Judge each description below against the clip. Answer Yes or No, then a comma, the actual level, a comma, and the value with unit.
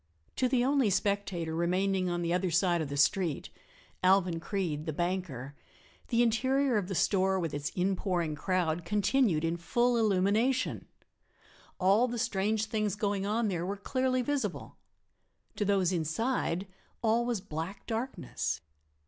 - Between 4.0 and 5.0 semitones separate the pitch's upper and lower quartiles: Yes, average, 4.5 semitones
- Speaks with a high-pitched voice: Yes, high, 195 Hz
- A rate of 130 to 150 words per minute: Yes, average, 145 wpm